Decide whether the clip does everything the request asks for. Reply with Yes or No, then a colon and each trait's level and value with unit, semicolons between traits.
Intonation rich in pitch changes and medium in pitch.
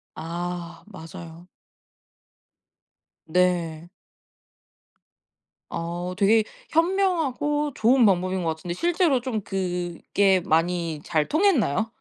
Yes: wide, 6.4 semitones; medium, 180 Hz